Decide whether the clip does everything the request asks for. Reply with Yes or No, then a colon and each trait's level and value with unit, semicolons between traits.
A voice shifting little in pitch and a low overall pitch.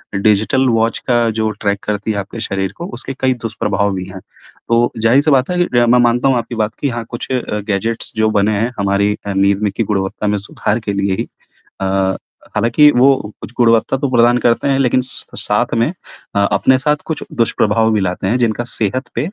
No: average, 3.3 semitones; low, 115 Hz